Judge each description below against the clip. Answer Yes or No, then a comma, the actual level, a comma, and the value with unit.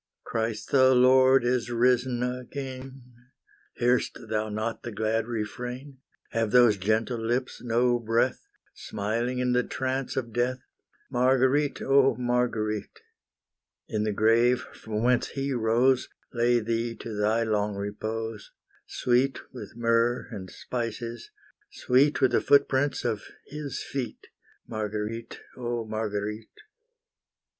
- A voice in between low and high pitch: No, low, 120 Hz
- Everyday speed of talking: No, slow, 120 wpm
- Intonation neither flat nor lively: No, narrow, 2.3 semitones